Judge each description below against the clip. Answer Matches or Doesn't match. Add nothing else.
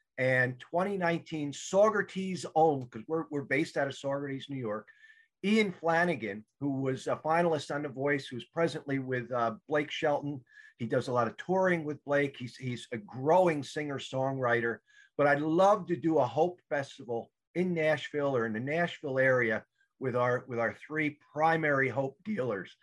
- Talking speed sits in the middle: Matches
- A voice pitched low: Doesn't match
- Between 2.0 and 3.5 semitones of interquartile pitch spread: Doesn't match